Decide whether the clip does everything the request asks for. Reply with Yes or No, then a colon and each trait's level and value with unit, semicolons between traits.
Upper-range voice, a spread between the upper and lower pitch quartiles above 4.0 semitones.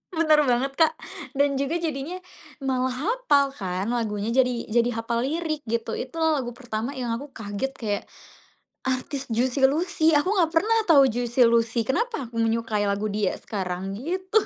Yes: very high, 255 Hz; average, 4.4 semitones